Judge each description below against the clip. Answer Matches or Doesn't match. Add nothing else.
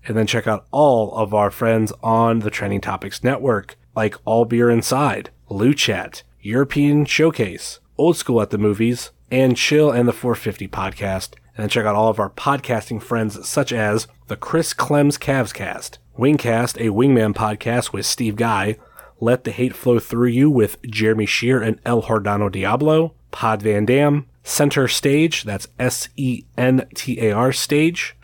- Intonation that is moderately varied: Matches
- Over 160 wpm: Matches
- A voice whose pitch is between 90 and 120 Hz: Matches